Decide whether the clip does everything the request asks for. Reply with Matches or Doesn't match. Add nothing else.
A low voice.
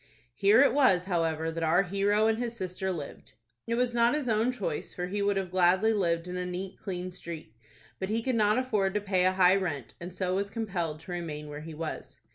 Doesn't match